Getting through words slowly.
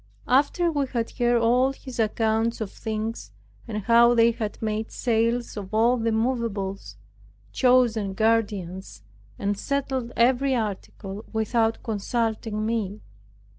Yes: slow, 125 wpm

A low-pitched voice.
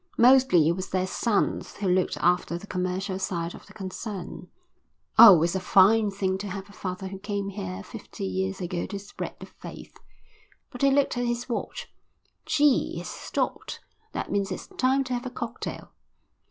No: high, 195 Hz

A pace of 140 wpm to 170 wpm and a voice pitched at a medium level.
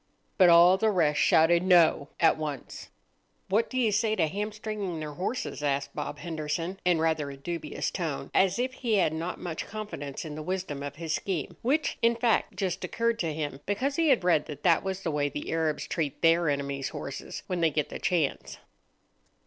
No: average, 200 wpm; medium, 170 Hz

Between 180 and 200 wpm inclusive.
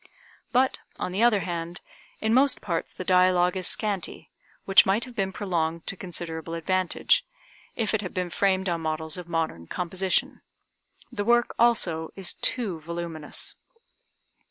No: average, 150 wpm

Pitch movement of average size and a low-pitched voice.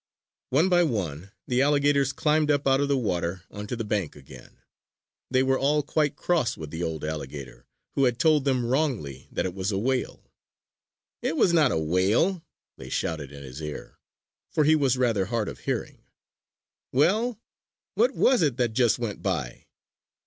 No: wide, 8.1 semitones; low, 125 Hz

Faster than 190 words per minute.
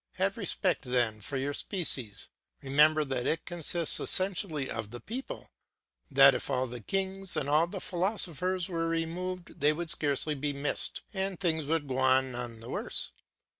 No: average, 170 wpm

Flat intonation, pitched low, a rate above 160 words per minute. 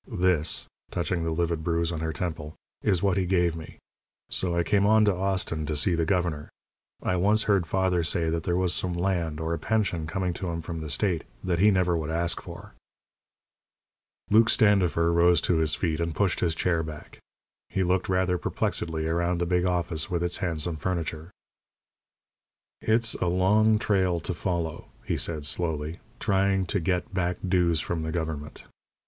Yes: narrow, 2.3 semitones; very low, 85 Hz; average, 180 wpm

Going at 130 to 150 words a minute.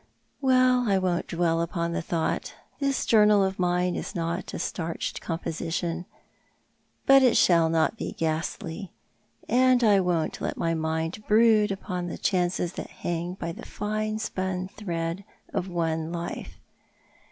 Yes: average, 140 wpm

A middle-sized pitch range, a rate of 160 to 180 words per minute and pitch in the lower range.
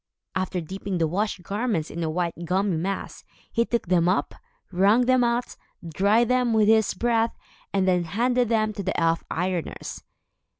No: average, 4.5 semitones; average, 170 wpm; high, 195 Hz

